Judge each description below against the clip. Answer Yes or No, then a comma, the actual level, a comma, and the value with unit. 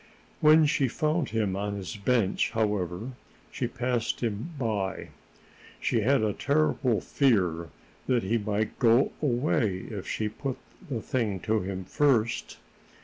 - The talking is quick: No, average, 140 wpm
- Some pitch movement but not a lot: Yes, average, 4.3 semitones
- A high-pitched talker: No, low, 115 Hz